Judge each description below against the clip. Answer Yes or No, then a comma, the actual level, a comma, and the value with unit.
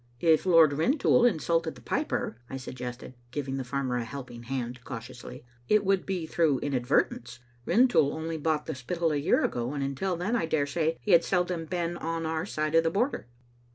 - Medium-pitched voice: Yes, medium, 155 Hz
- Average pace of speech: Yes, average, 190 wpm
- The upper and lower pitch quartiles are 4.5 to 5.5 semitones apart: Yes, average, 4.8 semitones